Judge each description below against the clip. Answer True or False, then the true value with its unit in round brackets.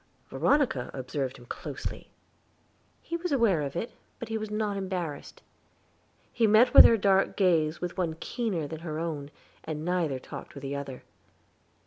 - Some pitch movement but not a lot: False (6.5 semitones)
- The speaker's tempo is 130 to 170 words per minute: True (150 wpm)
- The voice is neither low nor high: True (175 Hz)